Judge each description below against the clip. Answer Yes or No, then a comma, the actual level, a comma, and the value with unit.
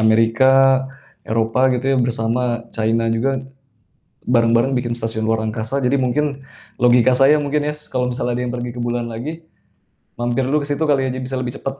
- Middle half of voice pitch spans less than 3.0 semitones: Yes, narrow, 2.5 semitones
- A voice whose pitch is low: Yes, low, 125 Hz